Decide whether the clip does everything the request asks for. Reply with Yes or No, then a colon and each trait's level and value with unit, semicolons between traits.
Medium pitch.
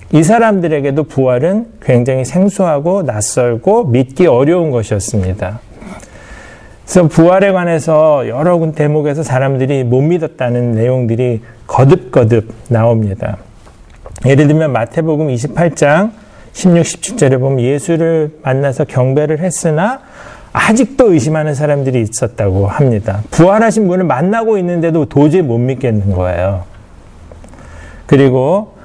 Yes: medium, 145 Hz